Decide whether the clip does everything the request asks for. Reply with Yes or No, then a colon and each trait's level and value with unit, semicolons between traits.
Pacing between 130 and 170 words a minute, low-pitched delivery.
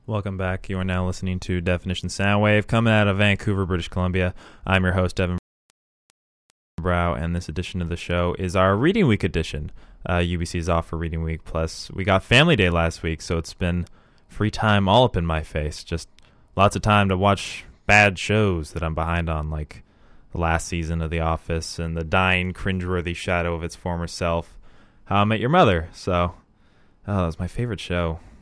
No: average, 200 wpm; very low, 90 Hz